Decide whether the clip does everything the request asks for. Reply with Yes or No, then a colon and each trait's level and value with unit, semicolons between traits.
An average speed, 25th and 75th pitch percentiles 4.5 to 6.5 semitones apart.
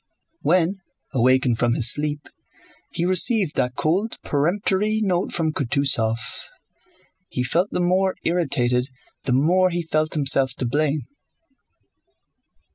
No: slow, 120 wpm; wide, 5.5 semitones